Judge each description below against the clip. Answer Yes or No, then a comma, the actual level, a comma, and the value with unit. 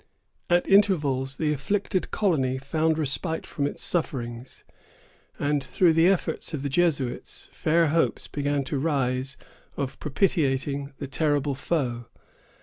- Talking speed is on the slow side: Yes, slow, 130 wpm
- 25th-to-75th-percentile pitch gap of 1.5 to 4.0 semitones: Yes, average, 3.4 semitones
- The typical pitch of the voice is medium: Yes, medium, 145 Hz